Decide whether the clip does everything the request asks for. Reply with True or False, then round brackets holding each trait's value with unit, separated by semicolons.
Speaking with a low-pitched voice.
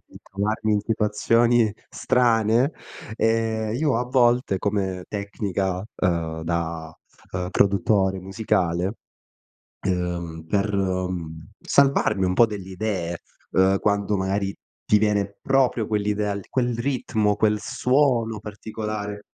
True (105 Hz)